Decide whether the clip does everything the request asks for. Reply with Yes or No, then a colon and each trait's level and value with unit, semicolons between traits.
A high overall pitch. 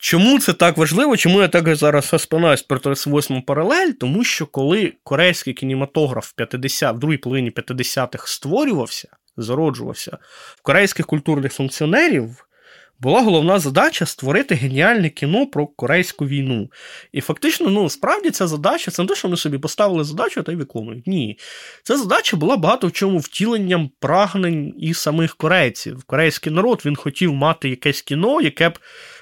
No: medium, 160 Hz